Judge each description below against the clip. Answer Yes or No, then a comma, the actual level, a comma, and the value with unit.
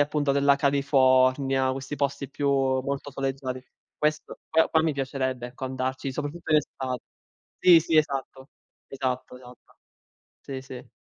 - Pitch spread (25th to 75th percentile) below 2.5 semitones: Yes, narrow, 1.5 semitones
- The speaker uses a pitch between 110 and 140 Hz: Yes, low, 135 Hz